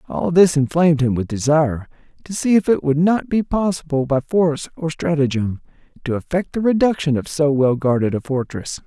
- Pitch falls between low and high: Yes, medium, 150 Hz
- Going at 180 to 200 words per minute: Yes, average, 190 wpm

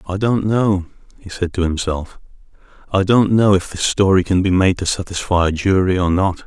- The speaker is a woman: No, male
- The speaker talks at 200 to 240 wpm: Yes, fast, 205 wpm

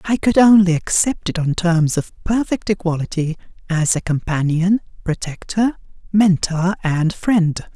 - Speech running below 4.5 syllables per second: Yes, 4.2 syllables/s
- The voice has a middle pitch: Yes, medium, 180 Hz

